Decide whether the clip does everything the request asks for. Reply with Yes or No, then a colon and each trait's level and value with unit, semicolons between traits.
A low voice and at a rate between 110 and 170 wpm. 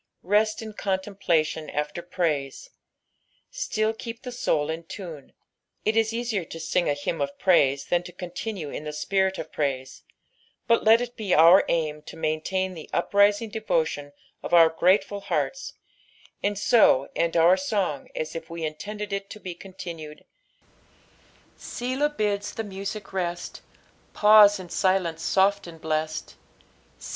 No: medium, 185 Hz; average, 150 wpm